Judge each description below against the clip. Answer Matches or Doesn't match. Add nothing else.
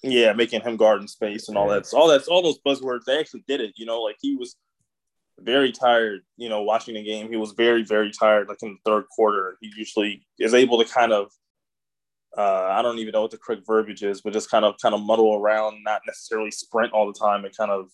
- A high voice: Doesn't match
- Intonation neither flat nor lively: Doesn't match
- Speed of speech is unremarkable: Doesn't match